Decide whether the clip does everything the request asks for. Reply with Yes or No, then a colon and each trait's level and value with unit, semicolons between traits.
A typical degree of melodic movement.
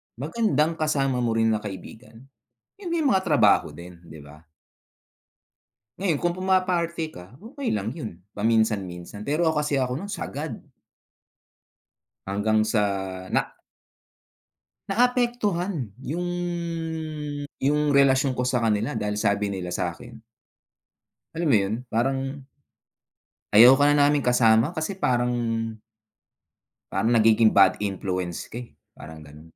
No: wide, 7.1 semitones